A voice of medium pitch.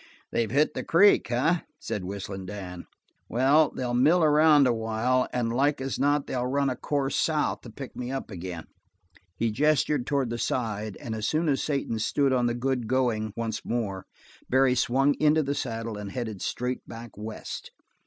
No: low, 125 Hz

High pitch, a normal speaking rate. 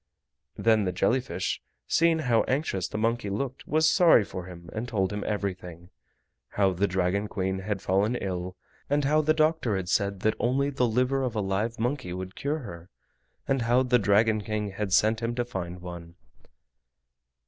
No: low, 105 Hz; average, 180 wpm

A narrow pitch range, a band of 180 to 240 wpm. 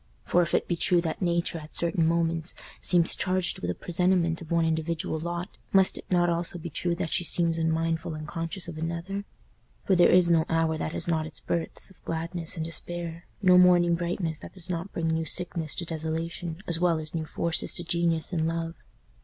Yes: narrow, 1.3 semitones; fast, 205 wpm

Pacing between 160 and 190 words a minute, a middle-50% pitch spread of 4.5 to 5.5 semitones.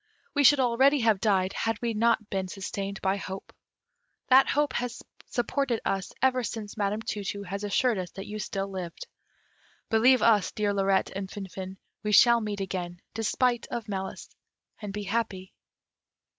No: average, 165 wpm; average, 3.2 semitones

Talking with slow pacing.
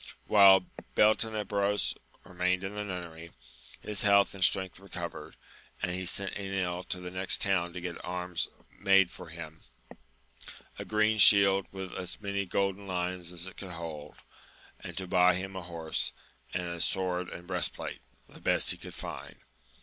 No: average, 160 wpm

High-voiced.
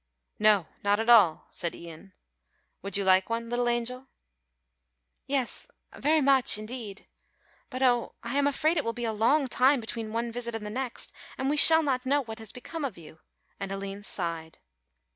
Yes: high, 235 Hz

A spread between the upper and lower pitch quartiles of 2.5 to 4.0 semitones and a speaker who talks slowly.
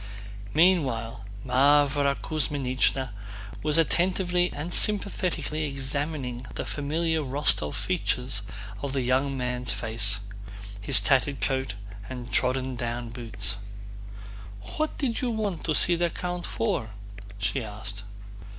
No: average, 4.7 semitones; slow, 115 wpm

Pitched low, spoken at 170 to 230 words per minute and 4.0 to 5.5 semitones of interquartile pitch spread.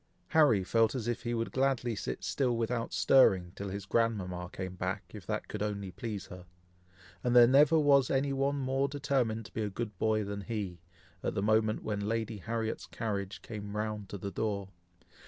No: low, 110 Hz; average, 195 wpm; average, 3.4 semitones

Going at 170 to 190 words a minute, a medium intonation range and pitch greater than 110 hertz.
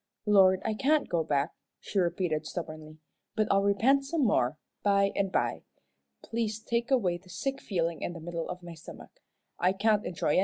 Yes: average, 185 wpm; average, 4.3 semitones; high, 190 Hz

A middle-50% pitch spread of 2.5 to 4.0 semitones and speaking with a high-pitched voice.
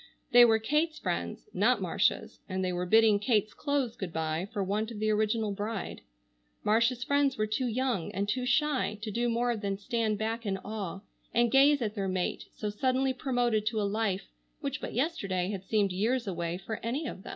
Yes: average, 3.5 semitones; high, 220 Hz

